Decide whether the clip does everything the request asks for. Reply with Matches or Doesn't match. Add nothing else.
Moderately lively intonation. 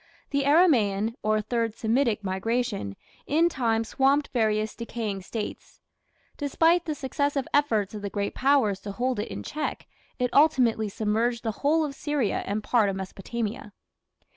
Matches